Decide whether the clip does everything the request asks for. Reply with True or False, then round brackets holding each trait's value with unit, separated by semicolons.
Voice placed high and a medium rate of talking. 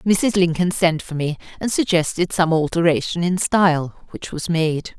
False (170 Hz; 170 wpm)